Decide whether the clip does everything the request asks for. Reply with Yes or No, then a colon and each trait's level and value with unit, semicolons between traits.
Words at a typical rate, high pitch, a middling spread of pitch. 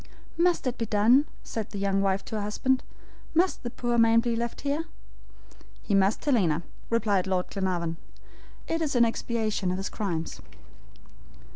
Yes: average, 160 wpm; high, 220 Hz; average, 3.9 semitones